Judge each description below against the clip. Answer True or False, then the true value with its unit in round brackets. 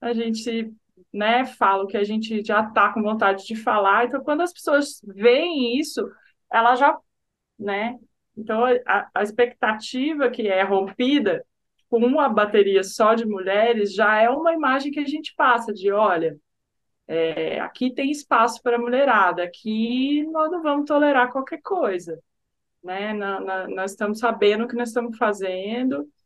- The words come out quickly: False (160 wpm)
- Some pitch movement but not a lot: True (4.3 semitones)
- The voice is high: True (225 Hz)